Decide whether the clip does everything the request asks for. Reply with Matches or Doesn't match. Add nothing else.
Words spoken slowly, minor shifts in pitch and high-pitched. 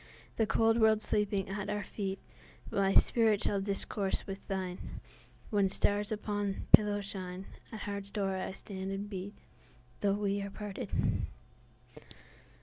Matches